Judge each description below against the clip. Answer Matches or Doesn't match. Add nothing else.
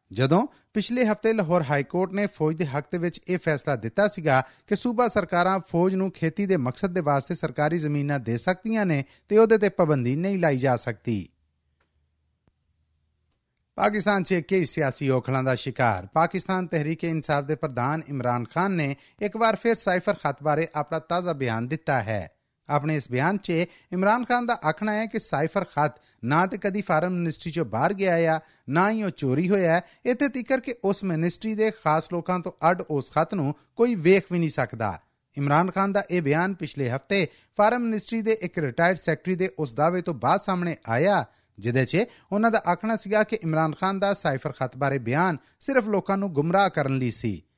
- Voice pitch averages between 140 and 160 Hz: Doesn't match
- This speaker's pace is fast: Matches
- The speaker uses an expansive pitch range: Matches